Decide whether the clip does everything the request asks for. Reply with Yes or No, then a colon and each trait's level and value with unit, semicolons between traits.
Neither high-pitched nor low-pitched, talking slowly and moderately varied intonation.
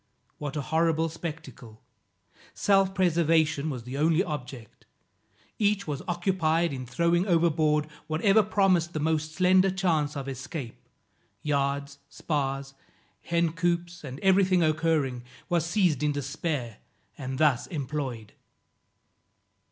Yes: medium, 155 Hz; slow, 115 wpm; average, 3.7 semitones